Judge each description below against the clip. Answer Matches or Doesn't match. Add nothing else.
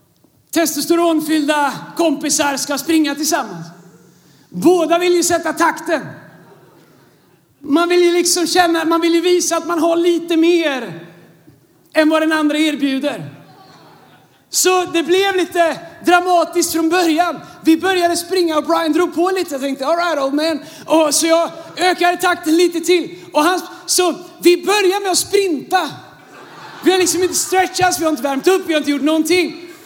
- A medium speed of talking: Matches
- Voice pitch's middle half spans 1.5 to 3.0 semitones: Matches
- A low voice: Doesn't match